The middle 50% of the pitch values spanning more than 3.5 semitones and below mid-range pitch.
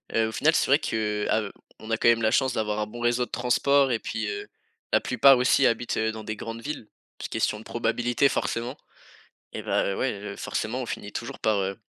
No: average, 2.7 semitones; low, 115 Hz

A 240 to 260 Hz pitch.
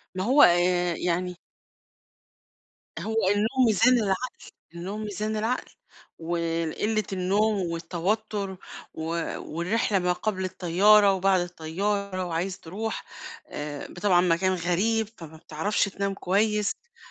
No: high, 190 Hz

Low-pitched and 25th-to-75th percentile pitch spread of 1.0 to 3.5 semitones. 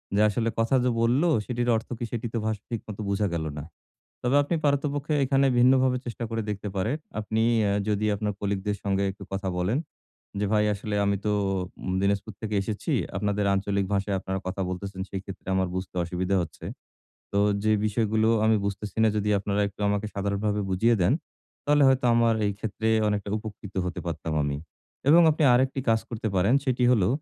Yes: low, 105 Hz; average, 2.9 semitones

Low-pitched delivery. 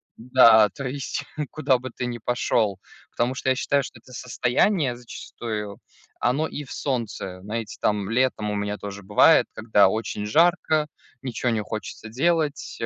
Yes: low, 120 Hz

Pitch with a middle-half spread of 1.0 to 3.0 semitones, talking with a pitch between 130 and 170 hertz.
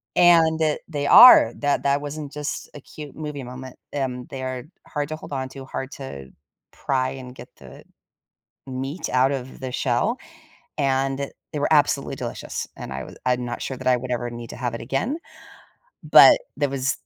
Yes: narrow, 2.4 semitones; low, 135 Hz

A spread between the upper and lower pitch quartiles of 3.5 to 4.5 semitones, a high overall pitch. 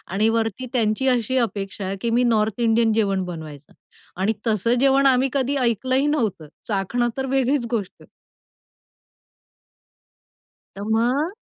Yes: average, 4.2 semitones; high, 230 Hz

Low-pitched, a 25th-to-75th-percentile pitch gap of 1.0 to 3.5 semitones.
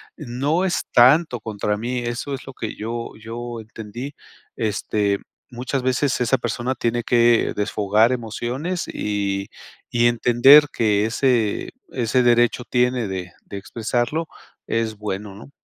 Yes: low, 120 Hz; average, 2.8 semitones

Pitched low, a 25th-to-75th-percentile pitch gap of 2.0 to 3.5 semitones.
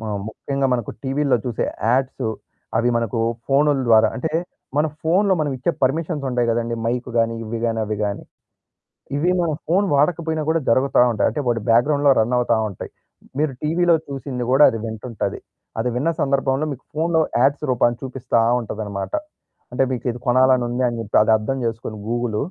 No: low, 130 Hz; average, 4.0 semitones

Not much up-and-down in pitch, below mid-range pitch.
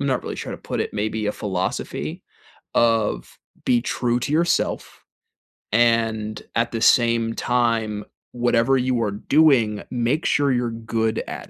Yes: narrow, 1.9 semitones; low, 115 Hz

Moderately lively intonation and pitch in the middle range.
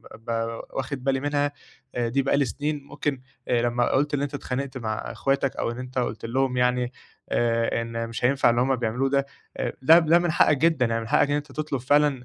No: average, 3.2 semitones; low, 130 Hz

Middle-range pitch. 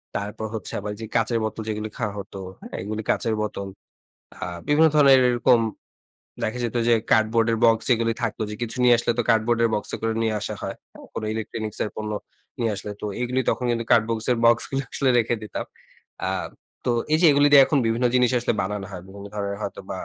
No: low, 115 Hz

